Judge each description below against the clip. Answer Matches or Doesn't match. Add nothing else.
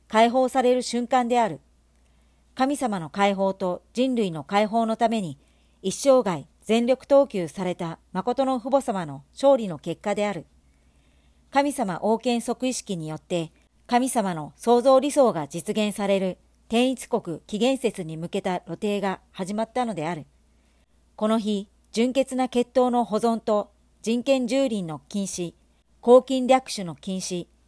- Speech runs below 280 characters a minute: Matches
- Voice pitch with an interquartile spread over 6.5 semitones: Doesn't match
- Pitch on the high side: Matches